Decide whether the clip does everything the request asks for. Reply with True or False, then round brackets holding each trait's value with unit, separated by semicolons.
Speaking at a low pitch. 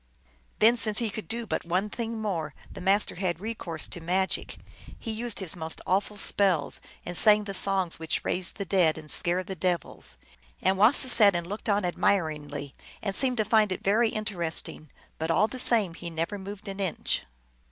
False (195 Hz)